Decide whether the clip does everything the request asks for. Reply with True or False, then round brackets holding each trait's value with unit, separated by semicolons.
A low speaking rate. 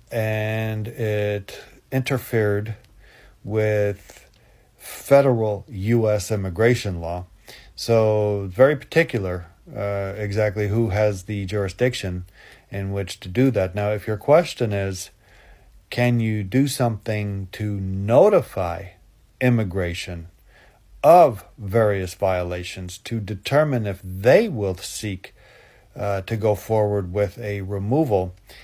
True (105 wpm)